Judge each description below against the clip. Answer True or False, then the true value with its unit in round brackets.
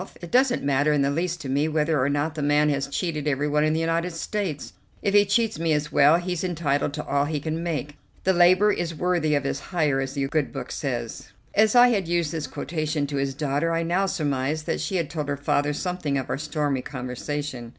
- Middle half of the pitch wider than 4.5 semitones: False (3.2 semitones)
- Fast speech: True (230 wpm)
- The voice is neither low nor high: True (150 Hz)